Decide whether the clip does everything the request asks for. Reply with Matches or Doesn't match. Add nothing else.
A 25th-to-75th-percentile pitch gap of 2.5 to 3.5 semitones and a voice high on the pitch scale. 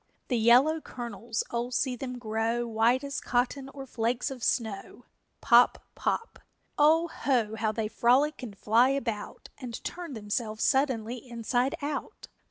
Matches